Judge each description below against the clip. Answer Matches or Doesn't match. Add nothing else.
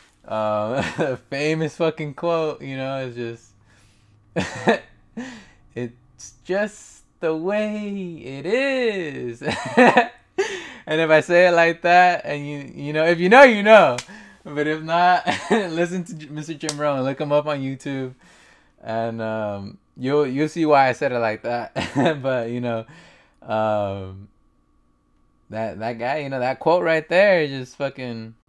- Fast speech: Doesn't match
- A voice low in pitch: Doesn't match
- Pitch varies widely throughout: Matches